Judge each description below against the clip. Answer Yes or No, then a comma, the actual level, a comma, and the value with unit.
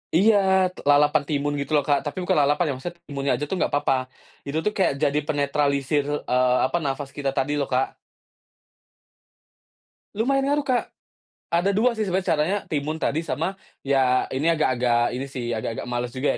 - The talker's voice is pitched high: No, medium, 145 Hz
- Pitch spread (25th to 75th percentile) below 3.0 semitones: No, average, 4.1 semitones